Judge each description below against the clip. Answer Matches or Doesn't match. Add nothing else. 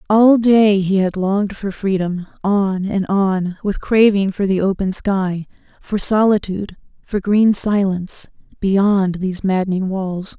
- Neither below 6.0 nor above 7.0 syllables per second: Doesn't match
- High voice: Matches